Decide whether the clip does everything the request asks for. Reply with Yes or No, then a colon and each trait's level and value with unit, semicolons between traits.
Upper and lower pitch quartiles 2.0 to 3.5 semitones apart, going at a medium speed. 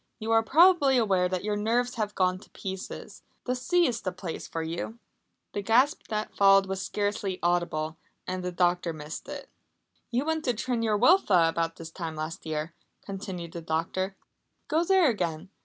No: wide, 5.5 semitones; average, 180 wpm